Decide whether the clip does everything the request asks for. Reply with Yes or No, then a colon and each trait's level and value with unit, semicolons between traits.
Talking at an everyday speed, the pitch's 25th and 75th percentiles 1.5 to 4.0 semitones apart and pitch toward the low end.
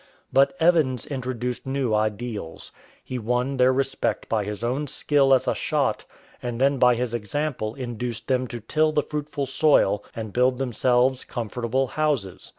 Yes: average, 155 wpm; average, 2.7 semitones; low, 125 Hz